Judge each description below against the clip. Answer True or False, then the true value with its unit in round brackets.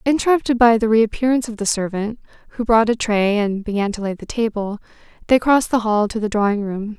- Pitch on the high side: True (220 Hz)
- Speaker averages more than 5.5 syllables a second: True (6.0 syllables/s)